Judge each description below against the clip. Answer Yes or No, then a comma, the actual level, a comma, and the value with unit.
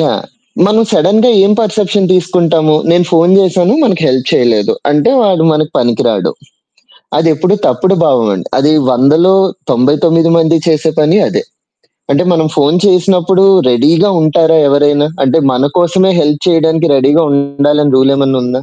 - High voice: No, medium, 160 Hz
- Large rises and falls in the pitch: No, average, 4.3 semitones